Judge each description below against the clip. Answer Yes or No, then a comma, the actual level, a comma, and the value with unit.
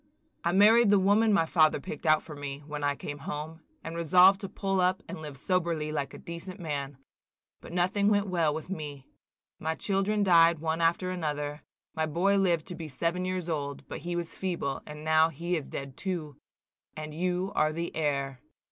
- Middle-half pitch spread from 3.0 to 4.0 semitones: Yes, average, 3.4 semitones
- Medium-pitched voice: Yes, medium, 165 Hz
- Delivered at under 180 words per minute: No, average, 195 wpm